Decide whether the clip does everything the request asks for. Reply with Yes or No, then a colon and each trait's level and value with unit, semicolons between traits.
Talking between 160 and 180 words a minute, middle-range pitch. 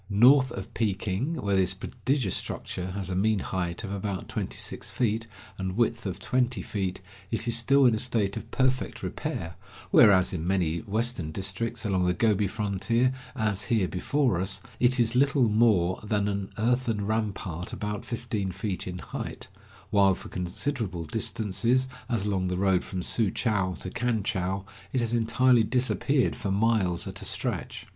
No: average, 170 wpm; low, 105 Hz